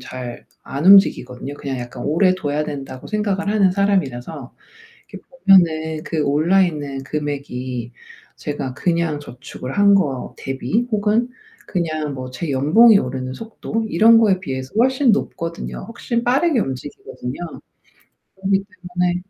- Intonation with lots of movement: Yes, wide, 6.8 semitones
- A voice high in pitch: No, medium, 165 Hz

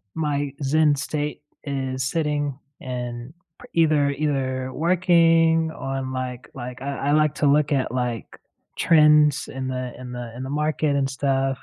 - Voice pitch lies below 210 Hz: Yes, medium, 140 Hz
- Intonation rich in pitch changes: No, narrow, 2.6 semitones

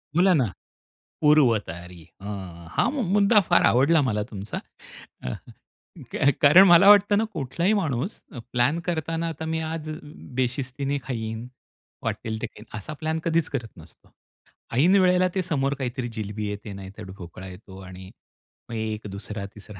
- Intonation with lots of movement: Yes, wide, 7.7 semitones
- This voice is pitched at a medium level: No, low, 125 Hz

